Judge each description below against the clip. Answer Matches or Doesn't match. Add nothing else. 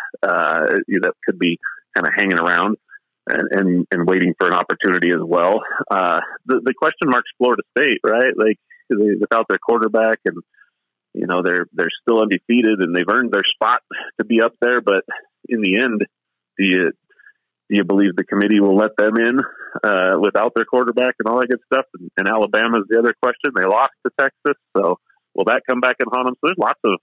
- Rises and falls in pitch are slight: Doesn't match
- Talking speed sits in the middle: Doesn't match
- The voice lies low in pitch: Matches